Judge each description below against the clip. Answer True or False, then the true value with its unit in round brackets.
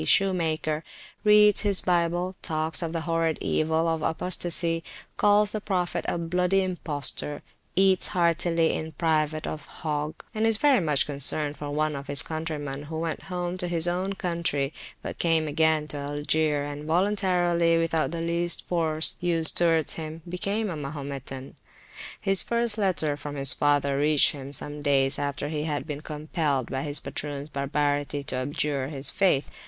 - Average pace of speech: True (160 wpm)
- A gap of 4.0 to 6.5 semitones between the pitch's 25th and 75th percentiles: False (3.1 semitones)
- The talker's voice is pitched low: False (160 Hz)